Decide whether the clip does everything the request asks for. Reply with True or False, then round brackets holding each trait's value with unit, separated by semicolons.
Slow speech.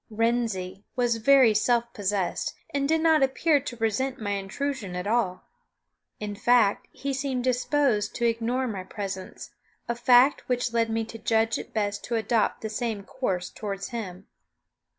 False (160 wpm)